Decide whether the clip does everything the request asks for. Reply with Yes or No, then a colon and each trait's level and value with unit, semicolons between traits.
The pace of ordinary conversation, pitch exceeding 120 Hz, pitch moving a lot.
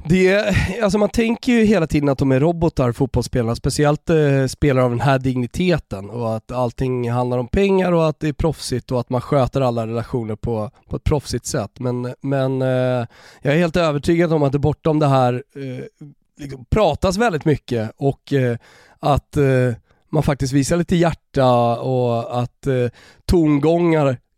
No: average, 175 wpm; low, 135 Hz; average, 4.1 semitones